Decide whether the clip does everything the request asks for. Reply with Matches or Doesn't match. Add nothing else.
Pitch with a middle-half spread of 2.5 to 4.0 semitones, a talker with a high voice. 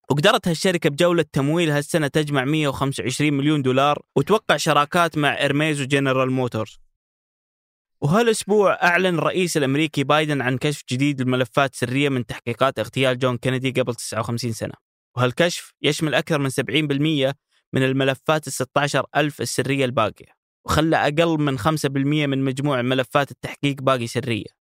Doesn't match